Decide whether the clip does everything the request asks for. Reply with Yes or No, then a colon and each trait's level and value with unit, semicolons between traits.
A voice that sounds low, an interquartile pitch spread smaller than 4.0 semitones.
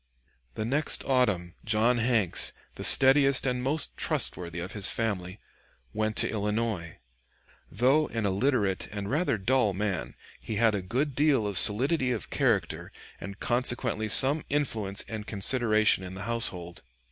No: low, 110 Hz; average, 4.5 semitones